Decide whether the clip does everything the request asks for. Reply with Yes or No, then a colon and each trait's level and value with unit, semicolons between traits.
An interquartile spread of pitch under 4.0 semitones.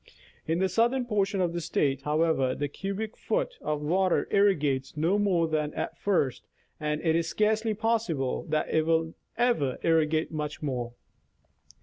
No: average, 5.1 semitones